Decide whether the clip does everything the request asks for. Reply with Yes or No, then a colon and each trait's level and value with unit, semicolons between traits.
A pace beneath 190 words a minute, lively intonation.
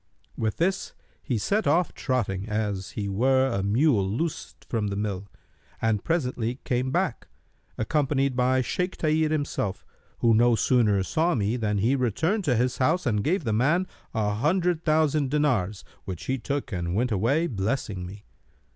Yes: average, 165 wpm; wide, 6.3 semitones